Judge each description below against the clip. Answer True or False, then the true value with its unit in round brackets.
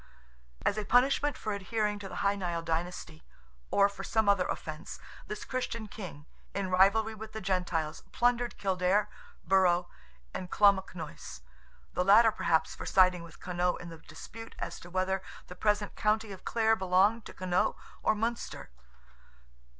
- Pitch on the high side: True (195 Hz)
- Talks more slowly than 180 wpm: True (150 wpm)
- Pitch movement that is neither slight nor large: True (3.2 semitones)